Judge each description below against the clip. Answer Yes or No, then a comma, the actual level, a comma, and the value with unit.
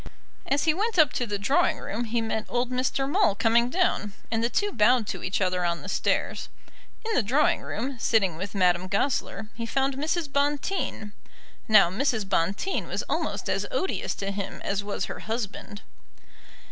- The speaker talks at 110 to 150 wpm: No, average, 180 wpm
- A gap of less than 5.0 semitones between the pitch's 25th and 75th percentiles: No, wide, 5.6 semitones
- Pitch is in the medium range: No, high, 230 Hz